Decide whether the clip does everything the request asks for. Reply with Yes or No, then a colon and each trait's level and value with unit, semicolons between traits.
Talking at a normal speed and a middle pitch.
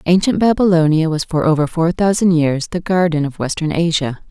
Yes: average, 180 wpm; medium, 165 Hz